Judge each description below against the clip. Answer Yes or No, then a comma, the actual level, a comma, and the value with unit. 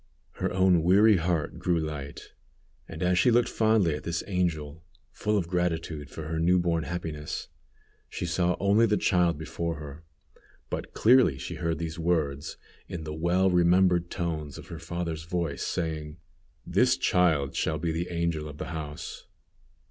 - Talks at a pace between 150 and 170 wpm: Yes, average, 165 wpm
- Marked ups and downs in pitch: No, narrow, 2.4 semitones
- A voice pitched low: Yes, very low, 85 Hz